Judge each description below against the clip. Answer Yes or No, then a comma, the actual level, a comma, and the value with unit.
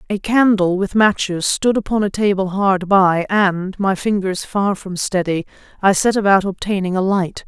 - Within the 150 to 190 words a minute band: Yes, average, 175 wpm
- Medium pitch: No, high, 195 Hz